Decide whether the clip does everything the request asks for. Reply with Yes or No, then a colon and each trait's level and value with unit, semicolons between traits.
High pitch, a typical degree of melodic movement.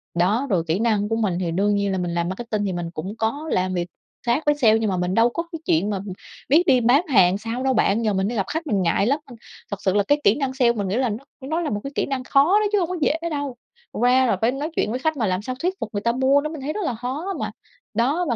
No: high, 235 Hz; wide, 5.7 semitones